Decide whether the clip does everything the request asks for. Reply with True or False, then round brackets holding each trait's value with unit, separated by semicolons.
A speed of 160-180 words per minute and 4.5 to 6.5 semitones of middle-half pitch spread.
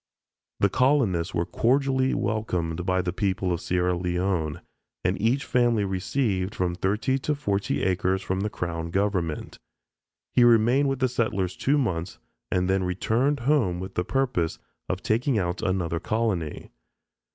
False (150 wpm; 5.1 semitones)